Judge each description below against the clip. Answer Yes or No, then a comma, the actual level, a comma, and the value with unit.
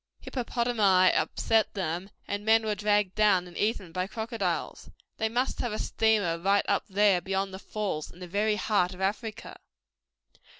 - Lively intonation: No, average, 2.8 semitones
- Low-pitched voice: No, high, 205 Hz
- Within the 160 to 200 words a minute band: Yes, average, 165 wpm